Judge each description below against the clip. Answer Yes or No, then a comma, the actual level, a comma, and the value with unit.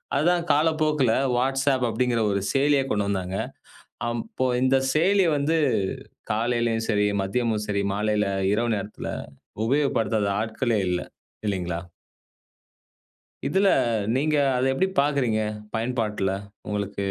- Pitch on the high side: No, low, 120 Hz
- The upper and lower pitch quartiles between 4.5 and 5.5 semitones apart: Yes, average, 5.0 semitones